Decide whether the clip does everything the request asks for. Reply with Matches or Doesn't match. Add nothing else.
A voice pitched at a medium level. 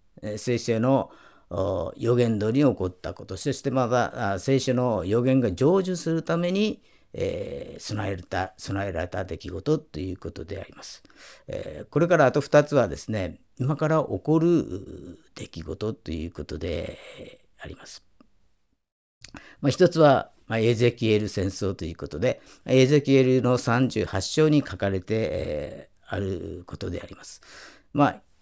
Doesn't match